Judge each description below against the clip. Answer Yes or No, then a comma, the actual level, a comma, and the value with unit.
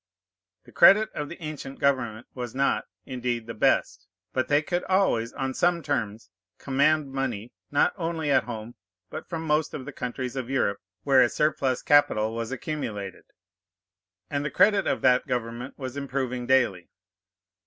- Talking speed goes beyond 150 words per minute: Yes, average, 160 wpm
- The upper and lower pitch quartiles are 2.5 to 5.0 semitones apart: Yes, average, 3.6 semitones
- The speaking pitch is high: No, low, 130 Hz